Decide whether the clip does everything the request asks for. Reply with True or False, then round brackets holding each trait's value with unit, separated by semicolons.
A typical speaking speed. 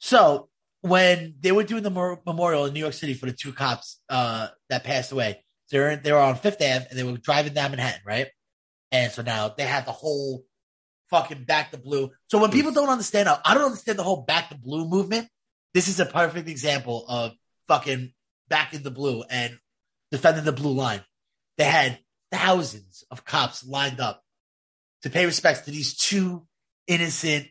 True (190 wpm)